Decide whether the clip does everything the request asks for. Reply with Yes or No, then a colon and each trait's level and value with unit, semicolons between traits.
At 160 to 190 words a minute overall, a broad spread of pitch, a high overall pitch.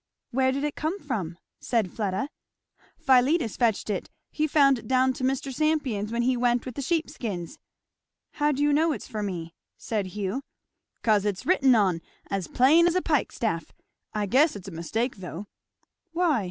Yes: average, 180 wpm; wide, 6.0 semitones; very high, 250 Hz